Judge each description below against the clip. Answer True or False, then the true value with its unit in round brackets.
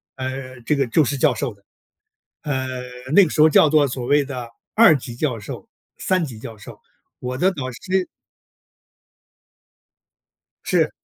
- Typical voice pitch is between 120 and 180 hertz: True (135 Hz)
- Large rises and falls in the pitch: False (3.8 semitones)